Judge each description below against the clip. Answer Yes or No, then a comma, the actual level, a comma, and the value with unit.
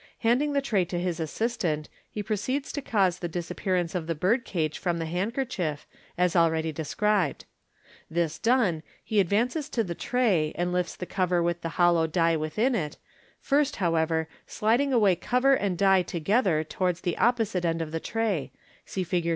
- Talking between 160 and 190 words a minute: Yes, average, 170 wpm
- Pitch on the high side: No, medium, 180 Hz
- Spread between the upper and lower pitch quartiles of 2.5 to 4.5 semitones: No, average, 5.3 semitones